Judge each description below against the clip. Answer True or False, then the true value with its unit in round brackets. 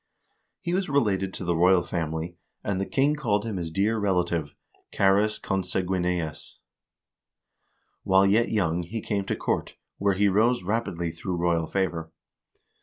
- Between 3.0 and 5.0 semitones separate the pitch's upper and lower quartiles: True (3.3 semitones)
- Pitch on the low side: True (95 Hz)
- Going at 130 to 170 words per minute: True (145 wpm)